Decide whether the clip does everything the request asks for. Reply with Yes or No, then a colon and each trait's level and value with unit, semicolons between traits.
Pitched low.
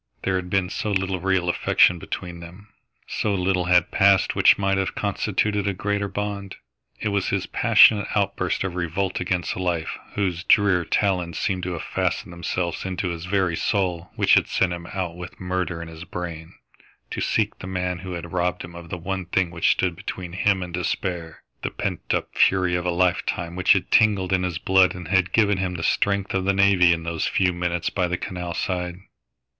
Yes: very low, 90 Hz